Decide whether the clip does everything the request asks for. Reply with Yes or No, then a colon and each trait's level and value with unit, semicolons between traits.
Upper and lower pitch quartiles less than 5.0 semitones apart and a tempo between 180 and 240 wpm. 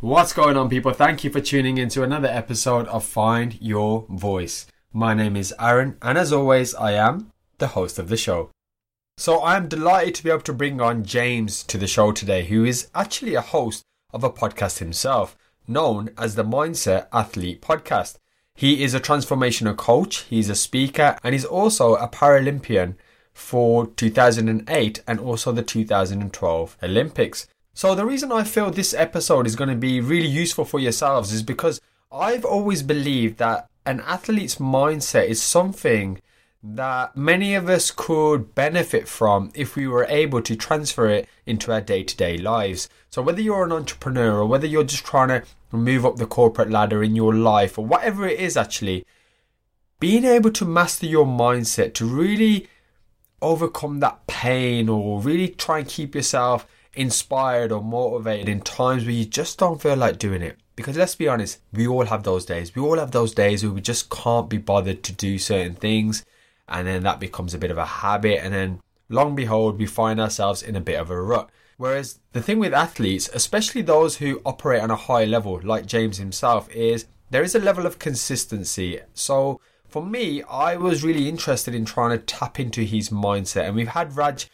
No: average, 5.3 semitones; average, 190 wpm